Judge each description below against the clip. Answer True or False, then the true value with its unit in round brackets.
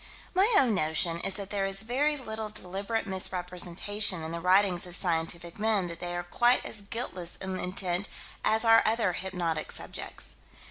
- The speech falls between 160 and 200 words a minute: True (170 wpm)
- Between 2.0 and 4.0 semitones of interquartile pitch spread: True (3.7 semitones)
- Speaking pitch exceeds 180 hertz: True (190 Hz)